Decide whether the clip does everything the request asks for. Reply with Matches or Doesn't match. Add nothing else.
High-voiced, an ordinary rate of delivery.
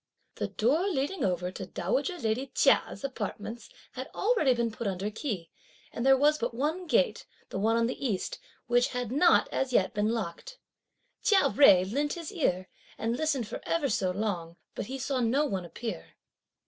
Matches